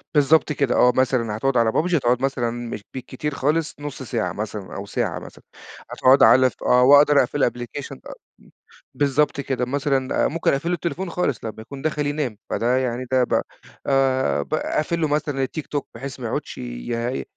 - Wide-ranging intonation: No, average, 3.2 semitones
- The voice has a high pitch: No, low, 135 Hz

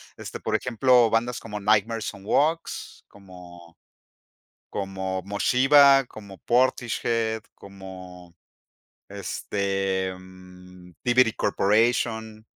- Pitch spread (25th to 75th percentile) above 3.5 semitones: Yes, average, 3.9 semitones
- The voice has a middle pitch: No, low, 100 Hz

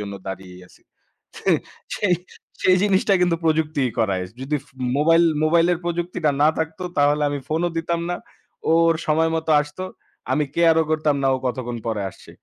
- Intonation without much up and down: No, average, 3.2 semitones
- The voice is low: No, medium, 155 Hz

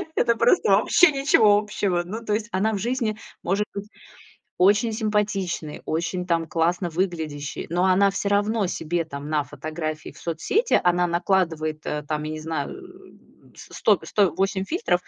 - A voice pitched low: No, medium, 185 Hz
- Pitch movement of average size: Yes, average, 4.4 semitones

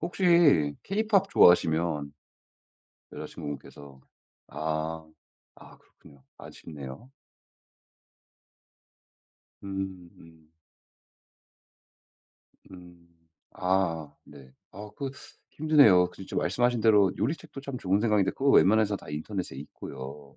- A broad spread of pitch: Yes, wide, 6.5 semitones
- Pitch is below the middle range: Yes, very low, 90 Hz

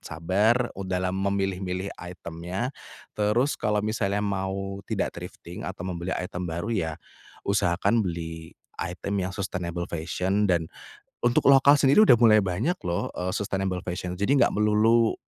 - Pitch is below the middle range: Yes, very low, 95 Hz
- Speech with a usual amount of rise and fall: Yes, average, 3.0 semitones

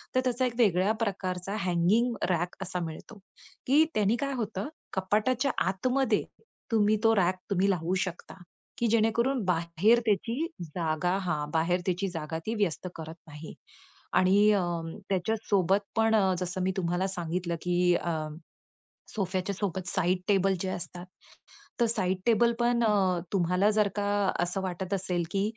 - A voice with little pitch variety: No, average, 3.4 semitones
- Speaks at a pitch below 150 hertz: No, high, 190 Hz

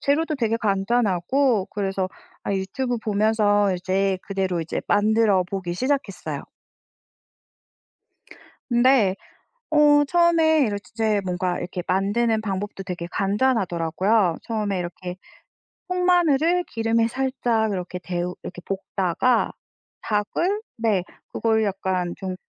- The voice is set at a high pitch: Yes, high, 205 Hz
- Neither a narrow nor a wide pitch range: Yes, average, 4.5 semitones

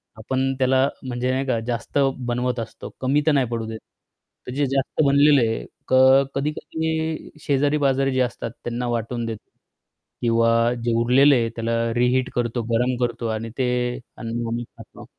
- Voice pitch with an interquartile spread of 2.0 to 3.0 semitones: Yes, narrow, 2.6 semitones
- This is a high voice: No, low, 125 Hz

